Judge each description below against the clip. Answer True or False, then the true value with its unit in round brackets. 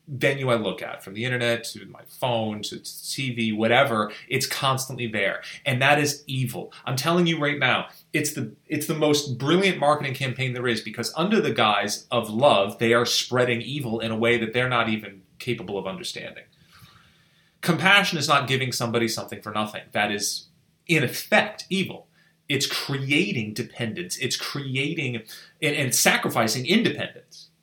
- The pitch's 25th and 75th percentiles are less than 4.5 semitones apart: True (4.0 semitones)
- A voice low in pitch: True (130 Hz)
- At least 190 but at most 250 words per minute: False (165 wpm)